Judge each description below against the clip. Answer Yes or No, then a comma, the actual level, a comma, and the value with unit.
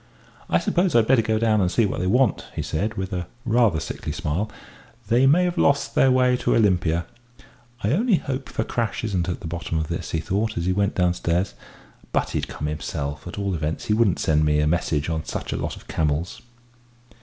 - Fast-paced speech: Yes, fast, 210 wpm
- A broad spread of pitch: Yes, wide, 6.2 semitones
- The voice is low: Yes, very low, 95 Hz